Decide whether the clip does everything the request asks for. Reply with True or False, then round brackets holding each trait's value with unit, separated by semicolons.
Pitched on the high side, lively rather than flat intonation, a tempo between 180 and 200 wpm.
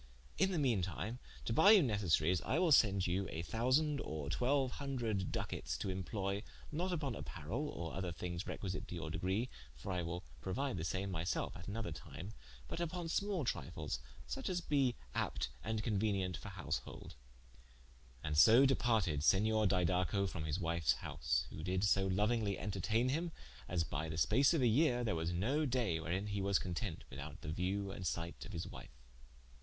False (100 Hz; 6.2 semitones; 185 wpm)